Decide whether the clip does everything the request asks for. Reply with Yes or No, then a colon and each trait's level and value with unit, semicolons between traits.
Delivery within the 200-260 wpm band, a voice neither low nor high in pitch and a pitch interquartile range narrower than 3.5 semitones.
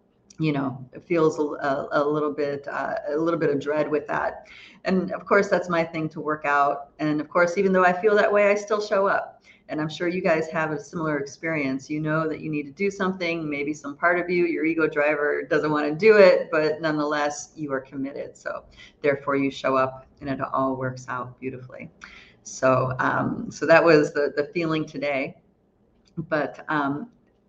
Yes: fast, 205 wpm; medium, 150 Hz; average, 2.9 semitones